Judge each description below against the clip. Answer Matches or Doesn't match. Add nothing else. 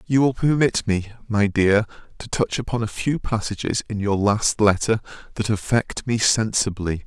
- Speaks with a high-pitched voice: Doesn't match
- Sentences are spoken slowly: Doesn't match